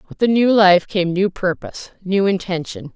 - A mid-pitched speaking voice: No, high, 195 Hz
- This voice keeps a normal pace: Yes, average, 185 wpm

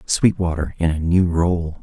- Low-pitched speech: Yes, very low, 85 Hz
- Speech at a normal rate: Yes, average, 165 wpm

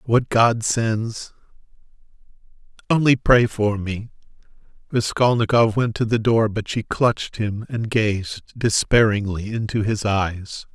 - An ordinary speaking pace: No, slow, 125 wpm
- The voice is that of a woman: No, male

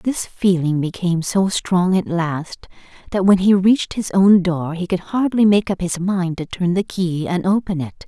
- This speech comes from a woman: Yes, female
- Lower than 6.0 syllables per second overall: Yes, 4.5 syllables/s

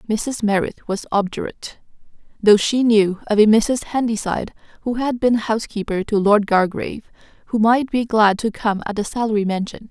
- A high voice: Yes, high, 215 Hz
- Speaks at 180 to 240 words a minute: No, average, 170 wpm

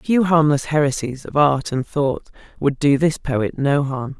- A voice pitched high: No, medium, 145 Hz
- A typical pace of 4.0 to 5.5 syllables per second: Yes, 4.5 syllables/s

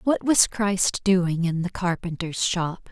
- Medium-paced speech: Yes, average, 165 wpm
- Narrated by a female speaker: Yes, female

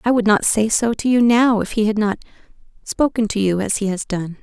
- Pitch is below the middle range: No, high, 215 Hz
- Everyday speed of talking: No, fast, 245 wpm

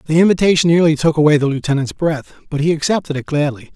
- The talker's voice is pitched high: No, medium, 155 Hz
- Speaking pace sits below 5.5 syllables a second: No, 6.7 syllables/s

